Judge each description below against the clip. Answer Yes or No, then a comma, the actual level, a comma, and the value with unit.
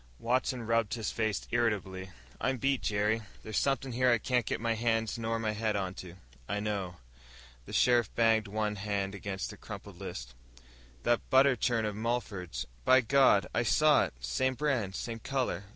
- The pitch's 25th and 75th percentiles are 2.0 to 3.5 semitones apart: Yes, average, 3.1 semitones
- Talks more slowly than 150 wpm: No, average, 175 wpm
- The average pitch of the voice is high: No, low, 115 Hz